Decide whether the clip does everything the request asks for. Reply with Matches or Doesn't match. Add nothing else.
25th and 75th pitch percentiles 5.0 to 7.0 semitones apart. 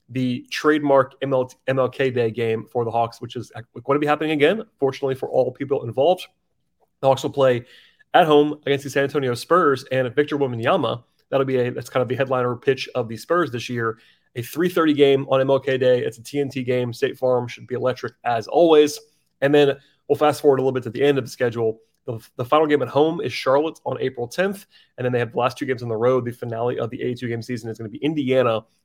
Doesn't match